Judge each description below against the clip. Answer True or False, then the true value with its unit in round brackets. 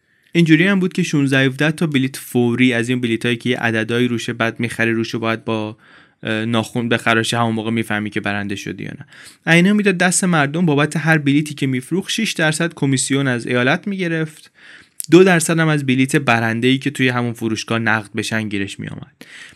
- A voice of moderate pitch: False (125 Hz)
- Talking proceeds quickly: True (195 wpm)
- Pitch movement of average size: False (5.8 semitones)